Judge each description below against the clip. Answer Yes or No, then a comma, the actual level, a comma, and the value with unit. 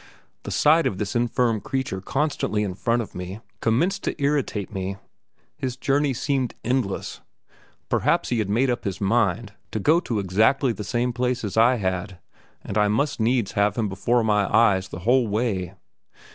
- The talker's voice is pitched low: Yes, low, 115 Hz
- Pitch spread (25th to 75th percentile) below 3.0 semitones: No, average, 4.2 semitones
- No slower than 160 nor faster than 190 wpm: Yes, average, 175 wpm